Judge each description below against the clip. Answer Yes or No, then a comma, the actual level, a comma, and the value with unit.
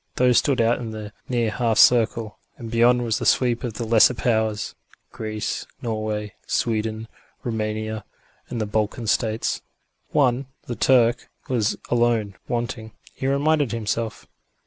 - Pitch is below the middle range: Yes, low, 115 Hz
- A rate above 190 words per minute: No, average, 140 wpm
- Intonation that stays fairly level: Yes, narrow, 1.9 semitones